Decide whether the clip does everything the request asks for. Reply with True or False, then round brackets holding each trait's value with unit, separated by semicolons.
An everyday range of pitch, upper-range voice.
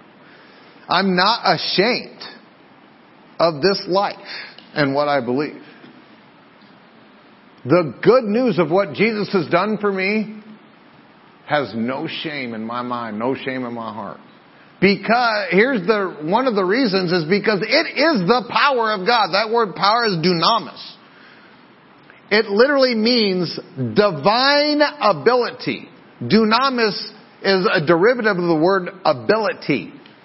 True (4.7 semitones; 200 Hz)